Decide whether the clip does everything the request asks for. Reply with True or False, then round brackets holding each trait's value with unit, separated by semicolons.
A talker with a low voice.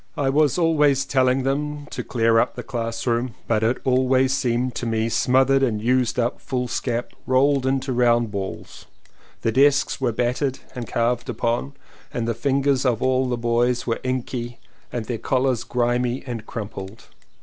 True (125 Hz)